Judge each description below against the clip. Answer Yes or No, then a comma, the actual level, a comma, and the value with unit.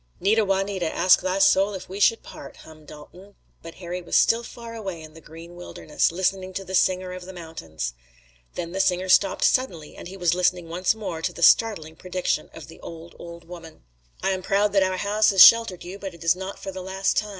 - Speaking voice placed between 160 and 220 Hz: Yes, medium, 185 Hz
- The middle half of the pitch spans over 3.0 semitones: No, narrow, 2.5 semitones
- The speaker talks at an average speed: No, fast, 225 wpm